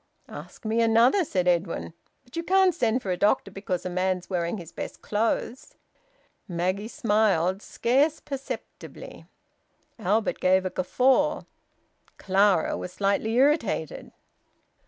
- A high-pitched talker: Yes, high, 210 Hz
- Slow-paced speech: Yes, slow, 125 wpm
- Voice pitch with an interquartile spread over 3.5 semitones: Yes, wide, 5.4 semitones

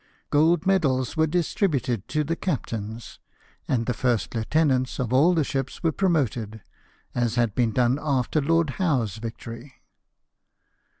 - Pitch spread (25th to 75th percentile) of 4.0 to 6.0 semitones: Yes, average, 5.2 semitones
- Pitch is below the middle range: Yes, low, 130 Hz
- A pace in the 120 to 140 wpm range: Yes, slow, 135 wpm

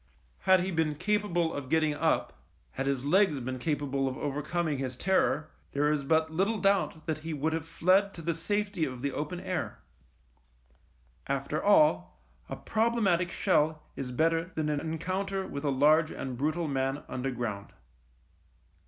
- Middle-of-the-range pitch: Yes, medium, 155 Hz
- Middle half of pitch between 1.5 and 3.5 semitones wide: No, average, 4.2 semitones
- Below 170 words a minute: Yes, average, 160 wpm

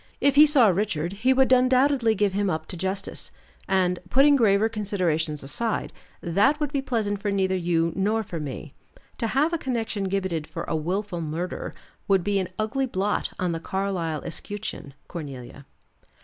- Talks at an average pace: Yes, average, 170 wpm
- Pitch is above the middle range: Yes, high, 195 Hz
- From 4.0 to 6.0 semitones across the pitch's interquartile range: Yes, average, 5.1 semitones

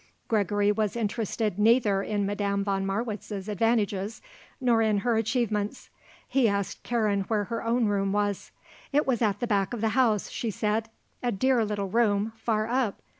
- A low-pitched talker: No, high, 215 Hz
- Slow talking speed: No, average, 170 wpm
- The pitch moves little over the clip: Yes, narrow, 2.3 semitones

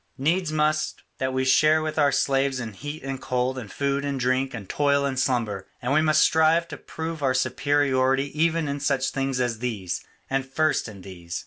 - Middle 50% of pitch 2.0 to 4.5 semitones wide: Yes, average, 2.9 semitones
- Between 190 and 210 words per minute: Yes, average, 200 wpm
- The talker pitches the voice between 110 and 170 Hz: Yes, low, 135 Hz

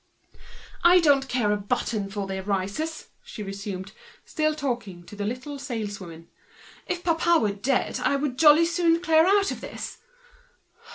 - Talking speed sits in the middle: Yes, average, 160 wpm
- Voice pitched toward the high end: Yes, very high, 250 Hz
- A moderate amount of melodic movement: No, wide, 8.0 semitones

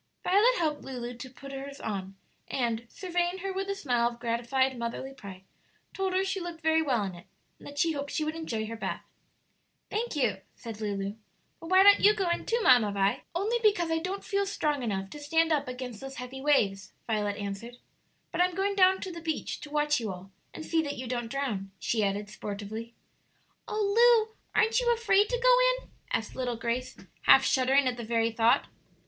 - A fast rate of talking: Yes, fast, 210 wpm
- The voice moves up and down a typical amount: No, wide, 8.2 semitones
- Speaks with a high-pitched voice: Yes, very high, 275 Hz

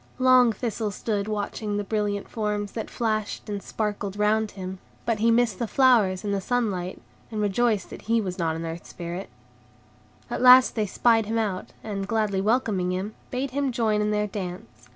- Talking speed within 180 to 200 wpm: Yes, average, 185 wpm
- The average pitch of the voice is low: No, high, 210 Hz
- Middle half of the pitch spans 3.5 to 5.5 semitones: No, average, 2.8 semitones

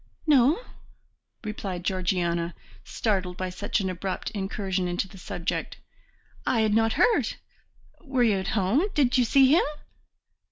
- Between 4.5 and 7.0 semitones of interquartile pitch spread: Yes, average, 4.8 semitones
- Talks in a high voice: Yes, high, 200 Hz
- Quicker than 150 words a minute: No, slow, 135 wpm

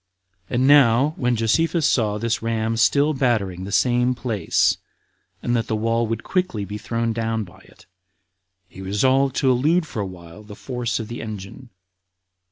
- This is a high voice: No, low, 115 Hz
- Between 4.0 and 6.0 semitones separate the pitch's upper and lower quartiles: No, average, 3.3 semitones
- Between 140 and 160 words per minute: No, average, 175 wpm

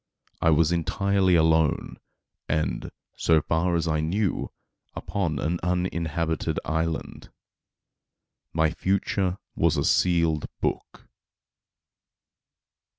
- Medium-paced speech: No, slow, 90 wpm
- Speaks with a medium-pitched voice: No, very low, 85 Hz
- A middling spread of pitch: No, narrow, 2.1 semitones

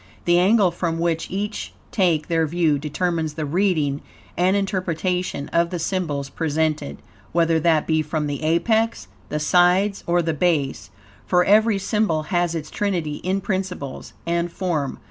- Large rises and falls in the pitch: No, average, 3.0 semitones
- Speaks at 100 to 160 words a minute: Yes, average, 150 wpm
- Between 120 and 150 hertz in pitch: No, medium, 170 Hz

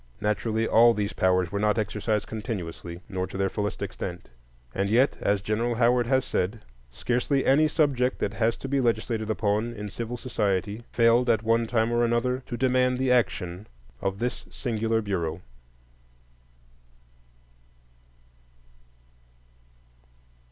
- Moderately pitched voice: No, low, 110 Hz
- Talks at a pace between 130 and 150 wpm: Yes, slow, 135 wpm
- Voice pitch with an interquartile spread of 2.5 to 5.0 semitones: Yes, average, 3.1 semitones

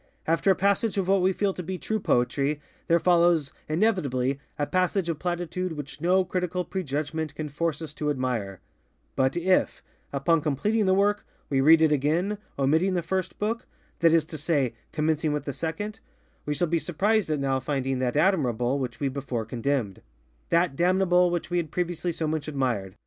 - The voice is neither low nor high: Yes, medium, 160 Hz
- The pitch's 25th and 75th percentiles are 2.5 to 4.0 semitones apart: No, average, 4.7 semitones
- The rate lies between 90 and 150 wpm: No, average, 175 wpm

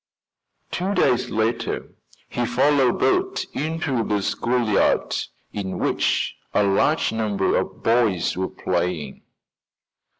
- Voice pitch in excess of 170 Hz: No, low, 115 Hz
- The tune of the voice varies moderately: No, wide, 5.7 semitones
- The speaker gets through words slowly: Yes, slow, 105 wpm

